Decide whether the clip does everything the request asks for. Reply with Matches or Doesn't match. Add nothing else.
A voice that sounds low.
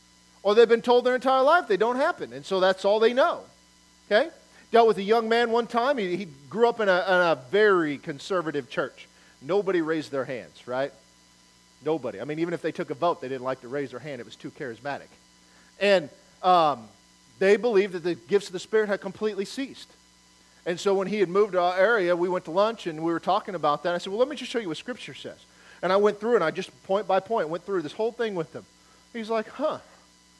Doesn't match